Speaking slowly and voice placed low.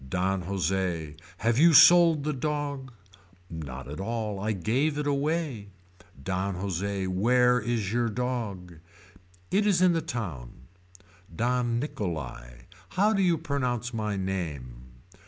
Yes: slow, 130 wpm; low, 110 Hz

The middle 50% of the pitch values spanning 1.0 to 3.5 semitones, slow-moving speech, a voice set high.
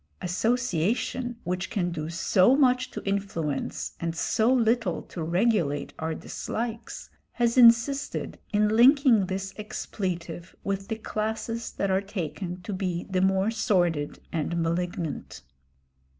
No: average, 4.9 semitones; slow, 125 wpm; high, 195 Hz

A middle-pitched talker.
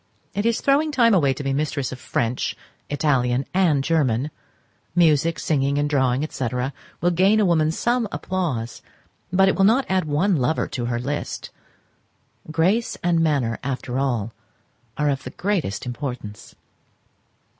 Yes: medium, 150 Hz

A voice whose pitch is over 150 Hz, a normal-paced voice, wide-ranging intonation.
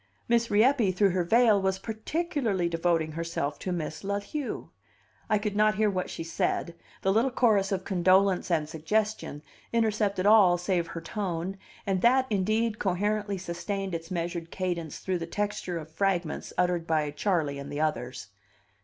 No: high, 190 Hz; average, 160 wpm; average, 3.9 semitones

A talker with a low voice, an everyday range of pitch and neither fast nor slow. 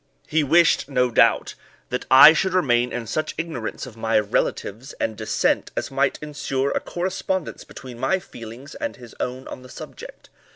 Yes: low, 130 Hz; average, 4.6 semitones; average, 170 wpm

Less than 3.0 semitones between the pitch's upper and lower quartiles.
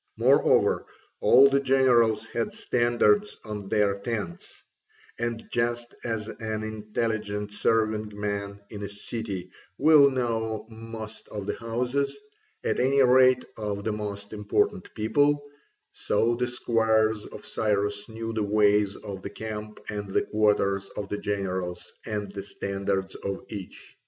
Yes: narrow, 2.5 semitones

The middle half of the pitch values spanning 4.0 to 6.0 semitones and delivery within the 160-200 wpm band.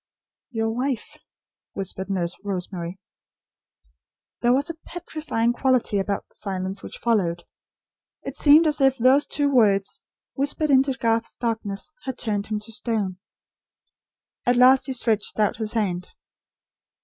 No: average, 4.8 semitones; slow, 135 wpm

